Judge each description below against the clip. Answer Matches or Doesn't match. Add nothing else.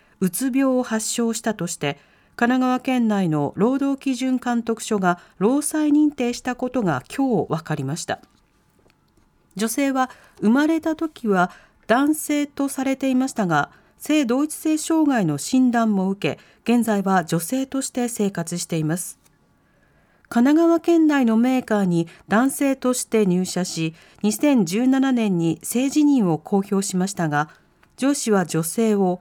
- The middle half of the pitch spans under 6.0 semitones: Doesn't match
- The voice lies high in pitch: Matches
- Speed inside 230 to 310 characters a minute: Matches